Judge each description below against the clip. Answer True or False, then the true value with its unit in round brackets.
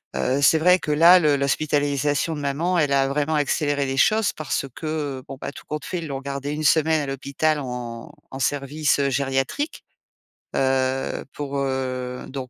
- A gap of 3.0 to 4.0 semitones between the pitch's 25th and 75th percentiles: False (2.4 semitones)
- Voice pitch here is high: False (140 Hz)